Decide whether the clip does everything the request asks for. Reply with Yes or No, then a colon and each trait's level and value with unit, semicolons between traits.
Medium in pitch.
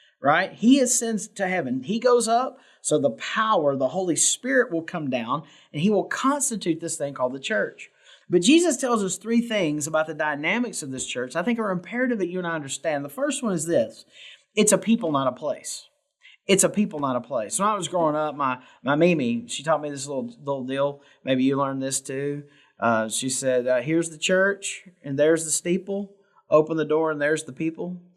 Yes: medium, 170 Hz